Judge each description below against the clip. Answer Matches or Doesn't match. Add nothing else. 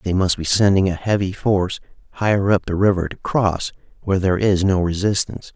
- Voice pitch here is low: Matches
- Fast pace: Doesn't match